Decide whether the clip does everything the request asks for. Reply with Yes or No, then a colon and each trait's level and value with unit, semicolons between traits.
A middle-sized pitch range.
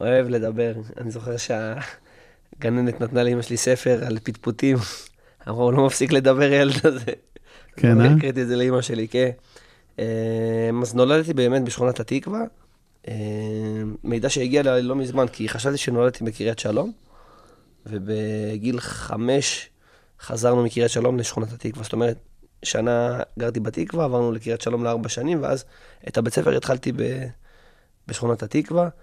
No: narrow, 2.3 semitones